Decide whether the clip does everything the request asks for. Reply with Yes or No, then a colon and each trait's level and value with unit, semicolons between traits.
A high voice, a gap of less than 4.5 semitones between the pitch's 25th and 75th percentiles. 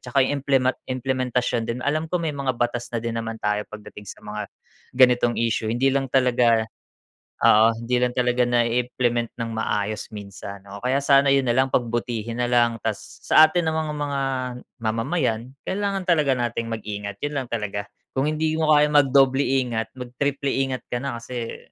No: low, 125 Hz; average, 3.2 semitones